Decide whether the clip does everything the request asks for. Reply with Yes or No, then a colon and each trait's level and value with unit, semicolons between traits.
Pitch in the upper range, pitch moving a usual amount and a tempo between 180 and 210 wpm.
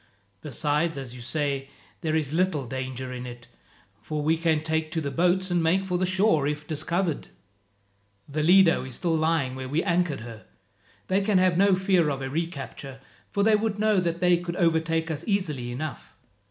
No: medium, 160 Hz; average, 4.4 semitones; average, 190 wpm